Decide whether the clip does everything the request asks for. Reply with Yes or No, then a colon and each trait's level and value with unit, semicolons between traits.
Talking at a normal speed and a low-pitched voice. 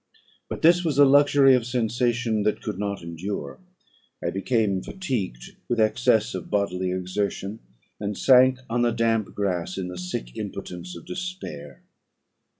Yes: average, 150 wpm; low, 105 Hz